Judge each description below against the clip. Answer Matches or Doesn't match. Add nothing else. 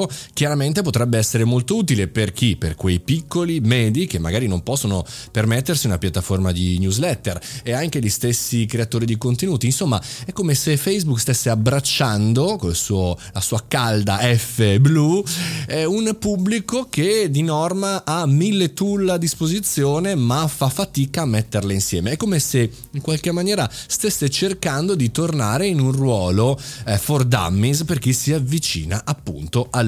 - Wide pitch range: Matches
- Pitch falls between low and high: Doesn't match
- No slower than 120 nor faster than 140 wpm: Doesn't match